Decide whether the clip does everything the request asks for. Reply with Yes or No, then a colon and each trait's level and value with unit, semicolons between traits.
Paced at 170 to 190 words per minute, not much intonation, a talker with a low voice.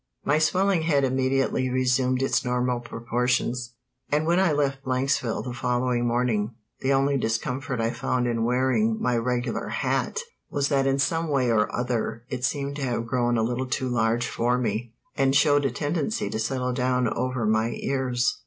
Yes: average, 175 wpm; narrow, 2.3 semitones; low, 125 Hz